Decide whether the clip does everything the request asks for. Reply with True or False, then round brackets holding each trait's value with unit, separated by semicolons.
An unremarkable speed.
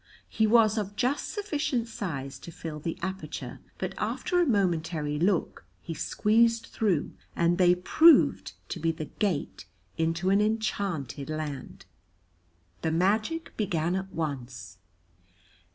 False (130 wpm)